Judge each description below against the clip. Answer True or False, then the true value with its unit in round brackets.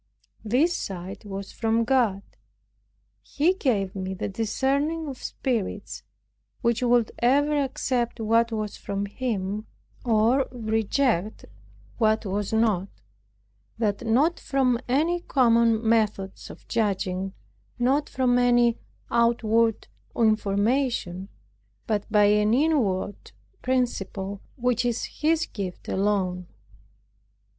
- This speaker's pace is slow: True (105 wpm)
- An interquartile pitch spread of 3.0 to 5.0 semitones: True (3.8 semitones)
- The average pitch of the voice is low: False (225 Hz)